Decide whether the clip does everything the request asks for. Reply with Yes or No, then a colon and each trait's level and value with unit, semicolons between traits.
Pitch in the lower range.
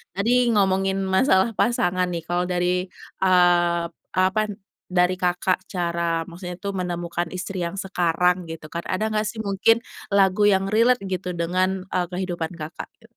No: medium, 180 Hz